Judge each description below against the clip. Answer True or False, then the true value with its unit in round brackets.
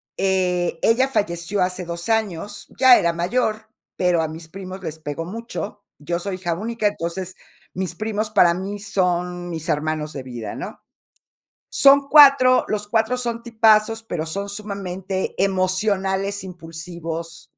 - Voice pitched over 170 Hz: True (190 Hz)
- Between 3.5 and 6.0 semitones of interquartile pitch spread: True (3.9 semitones)